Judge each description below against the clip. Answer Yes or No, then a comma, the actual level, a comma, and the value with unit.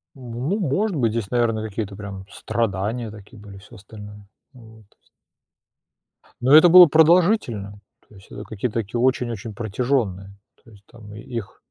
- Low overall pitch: Yes, low, 115 Hz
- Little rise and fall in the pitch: No, average, 3.6 semitones